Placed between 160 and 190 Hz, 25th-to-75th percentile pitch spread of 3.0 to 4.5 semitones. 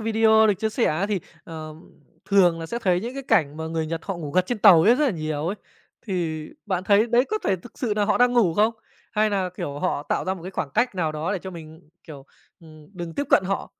No: medium, 185 Hz; average, 5.2 semitones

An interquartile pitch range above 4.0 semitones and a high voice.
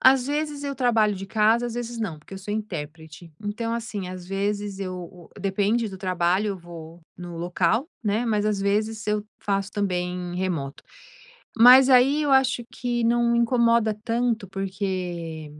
Yes: average, 4.4 semitones; high, 205 Hz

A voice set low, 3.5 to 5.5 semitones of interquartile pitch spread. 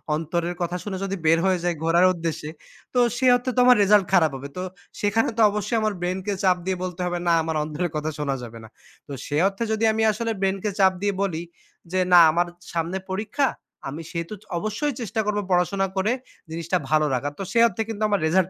No: medium, 185 Hz; average, 3.9 semitones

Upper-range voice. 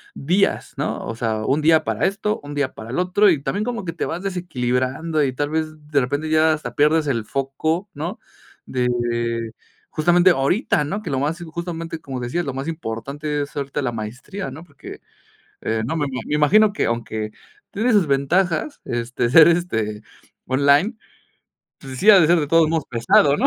No: medium, 150 Hz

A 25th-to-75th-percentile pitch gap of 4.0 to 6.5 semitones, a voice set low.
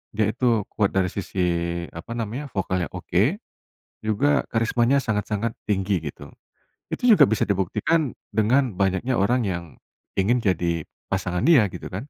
Yes: average, 4.4 semitones; low, 105 Hz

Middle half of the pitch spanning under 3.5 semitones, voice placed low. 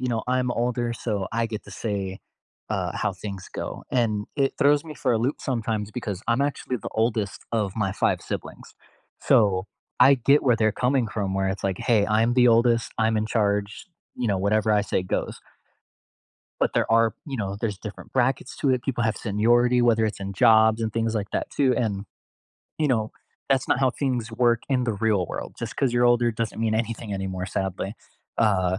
Yes: average, 2.9 semitones; low, 115 Hz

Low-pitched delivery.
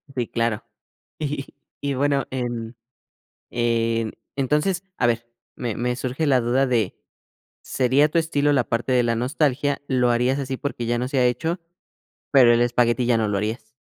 Yes: low, 125 Hz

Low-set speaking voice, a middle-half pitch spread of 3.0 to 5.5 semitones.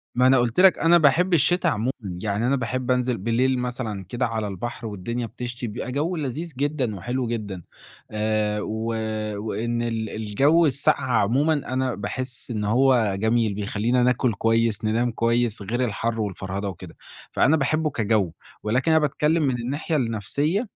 Yes: low, 120 Hz; average, 3.5 semitones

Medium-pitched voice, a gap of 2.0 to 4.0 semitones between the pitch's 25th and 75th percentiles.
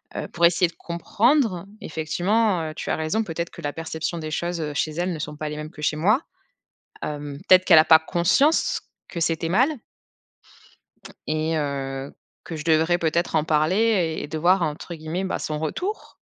Yes: medium, 165 Hz; narrow, 2.5 semitones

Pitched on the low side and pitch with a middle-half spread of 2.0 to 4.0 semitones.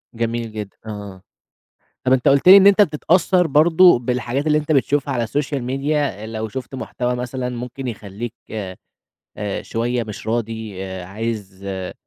No: low, 120 Hz; average, 4.5 semitones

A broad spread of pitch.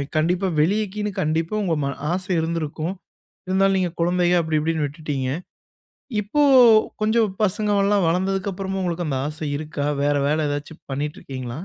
No: average, 4.2 semitones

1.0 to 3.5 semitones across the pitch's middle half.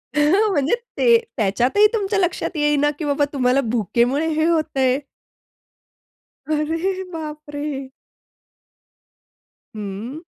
No: average, 4.0 semitones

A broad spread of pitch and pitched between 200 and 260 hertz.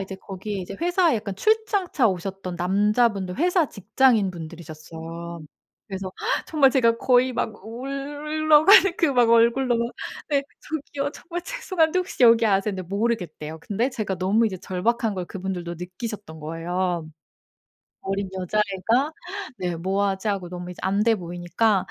Yes: wide, 6.0 semitones; high, 205 Hz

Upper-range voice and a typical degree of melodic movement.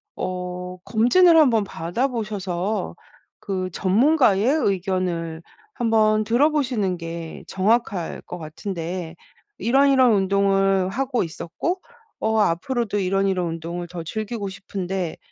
Yes: high, 195 Hz; average, 4.4 semitones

